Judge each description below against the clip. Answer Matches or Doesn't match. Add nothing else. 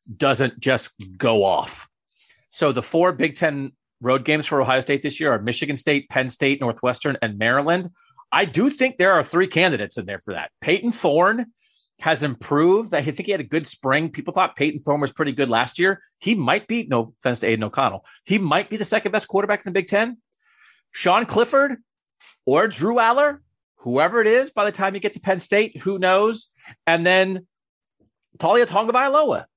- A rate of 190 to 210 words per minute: Matches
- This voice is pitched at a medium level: Matches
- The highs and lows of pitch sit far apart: Matches